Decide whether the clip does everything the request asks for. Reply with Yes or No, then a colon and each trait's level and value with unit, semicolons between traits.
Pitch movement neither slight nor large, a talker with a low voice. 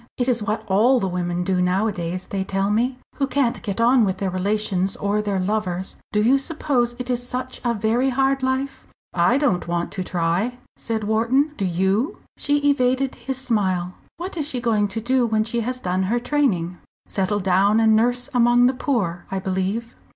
No: average, 4.8 semitones; high, 220 Hz